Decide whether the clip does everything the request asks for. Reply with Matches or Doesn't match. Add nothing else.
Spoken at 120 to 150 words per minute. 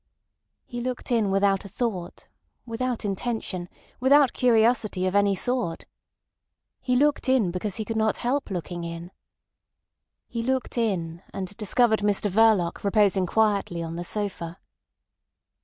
Matches